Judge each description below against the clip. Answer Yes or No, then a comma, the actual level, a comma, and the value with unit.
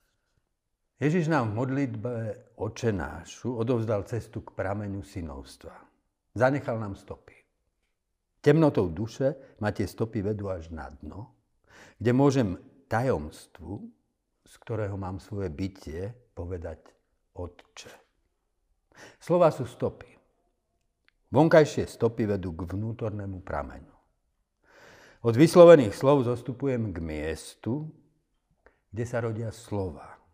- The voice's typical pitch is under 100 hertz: No, low, 110 Hz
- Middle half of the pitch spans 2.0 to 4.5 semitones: No, average, 5.2 semitones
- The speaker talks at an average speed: No, slow, 105 wpm